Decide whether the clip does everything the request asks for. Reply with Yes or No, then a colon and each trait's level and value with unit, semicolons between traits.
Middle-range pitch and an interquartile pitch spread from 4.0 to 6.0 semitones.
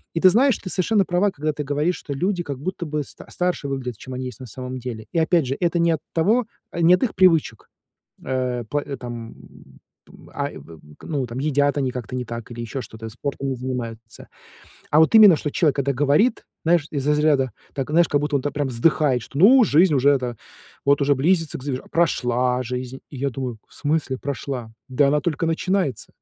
Yes: medium, 145 Hz; average, 4.5 semitones